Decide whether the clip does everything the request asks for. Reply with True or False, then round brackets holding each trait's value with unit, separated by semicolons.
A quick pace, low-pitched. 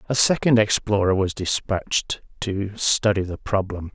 False (135 wpm; 100 Hz)